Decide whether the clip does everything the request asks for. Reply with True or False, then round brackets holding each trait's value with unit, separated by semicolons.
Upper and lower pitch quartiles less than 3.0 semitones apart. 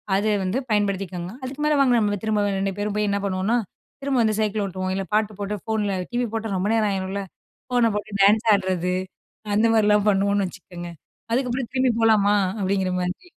True (2.4 semitones)